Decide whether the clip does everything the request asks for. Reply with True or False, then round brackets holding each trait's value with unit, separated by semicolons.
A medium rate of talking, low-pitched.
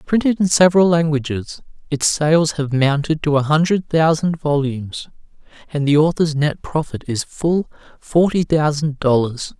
False (145 wpm; 155 Hz)